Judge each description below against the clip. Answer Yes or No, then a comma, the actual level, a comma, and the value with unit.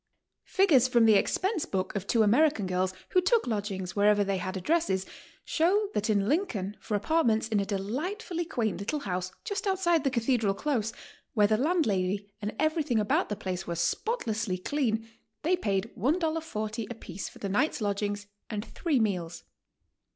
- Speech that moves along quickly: No, average, 175 wpm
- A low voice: No, high, 220 Hz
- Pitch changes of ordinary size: No, wide, 7.7 semitones